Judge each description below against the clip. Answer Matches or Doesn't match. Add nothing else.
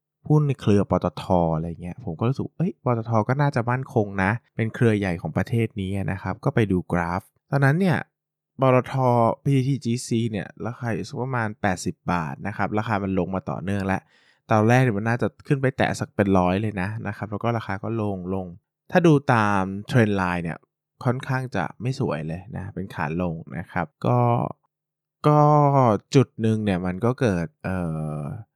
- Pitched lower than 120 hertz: Matches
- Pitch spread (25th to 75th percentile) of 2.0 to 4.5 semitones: Doesn't match